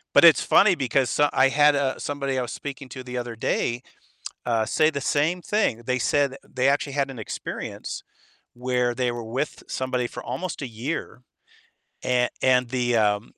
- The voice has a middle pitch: No, low, 130 Hz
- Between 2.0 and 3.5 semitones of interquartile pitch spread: Yes, average, 2.7 semitones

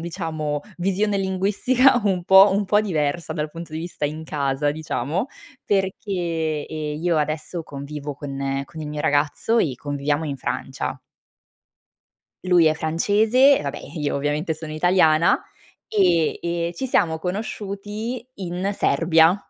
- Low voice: No, medium, 165 Hz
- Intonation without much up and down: No, average, 4.2 semitones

